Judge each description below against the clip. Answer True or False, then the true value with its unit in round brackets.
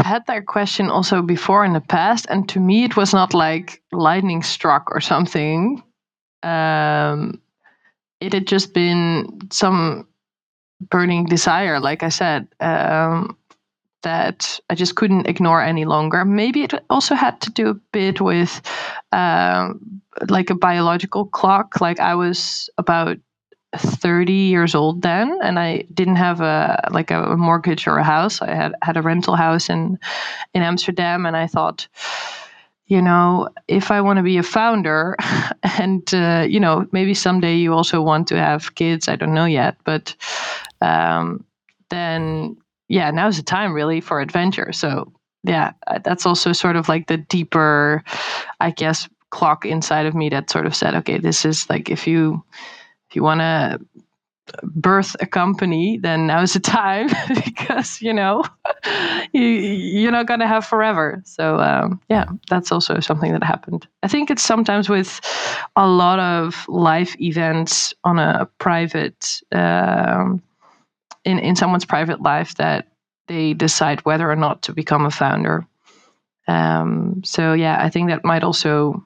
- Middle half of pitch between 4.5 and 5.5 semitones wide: False (3.3 semitones)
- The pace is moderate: True (160 wpm)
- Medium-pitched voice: True (175 Hz)